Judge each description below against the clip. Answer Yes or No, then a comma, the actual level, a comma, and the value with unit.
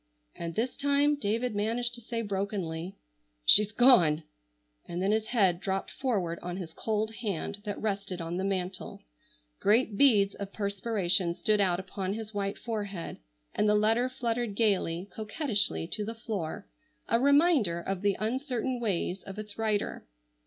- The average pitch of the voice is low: No, high, 205 Hz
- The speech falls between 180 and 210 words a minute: No, average, 155 wpm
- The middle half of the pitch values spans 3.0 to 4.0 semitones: Yes, average, 3.4 semitones